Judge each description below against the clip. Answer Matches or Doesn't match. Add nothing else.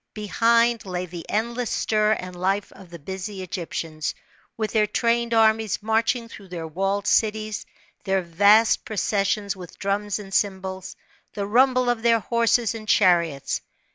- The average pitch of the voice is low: Doesn't match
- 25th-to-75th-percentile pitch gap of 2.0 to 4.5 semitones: Matches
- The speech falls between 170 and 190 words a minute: Doesn't match